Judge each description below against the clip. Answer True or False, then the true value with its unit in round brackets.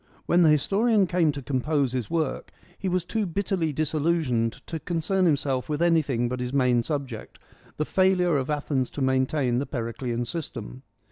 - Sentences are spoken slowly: False (175 wpm)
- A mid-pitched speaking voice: True (150 Hz)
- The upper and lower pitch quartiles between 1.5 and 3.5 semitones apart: False (4.9 semitones)